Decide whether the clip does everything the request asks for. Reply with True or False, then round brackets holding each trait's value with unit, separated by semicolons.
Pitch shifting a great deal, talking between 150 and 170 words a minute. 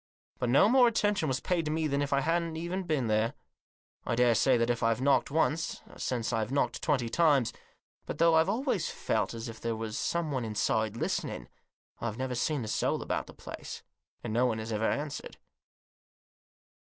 False (5.8 semitones; 185 wpm)